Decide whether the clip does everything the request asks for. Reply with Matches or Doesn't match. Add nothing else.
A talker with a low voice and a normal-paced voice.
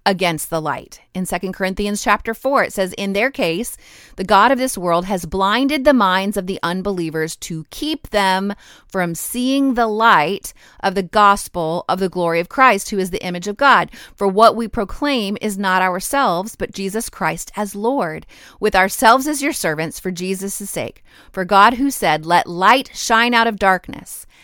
Doesn't match